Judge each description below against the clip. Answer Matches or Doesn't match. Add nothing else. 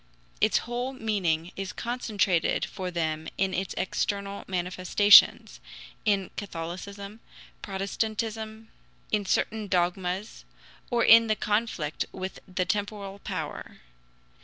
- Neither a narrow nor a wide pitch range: Matches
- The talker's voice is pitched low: Doesn't match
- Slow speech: Matches